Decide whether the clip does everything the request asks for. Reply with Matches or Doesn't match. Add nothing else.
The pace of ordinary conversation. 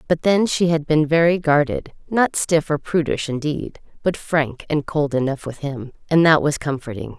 Matches